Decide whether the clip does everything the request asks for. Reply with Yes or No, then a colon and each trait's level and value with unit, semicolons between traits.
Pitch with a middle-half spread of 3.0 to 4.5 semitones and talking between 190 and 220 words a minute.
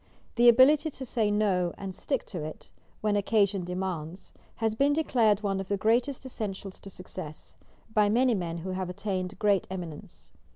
No: average, 3.6 semitones; average, 170 wpm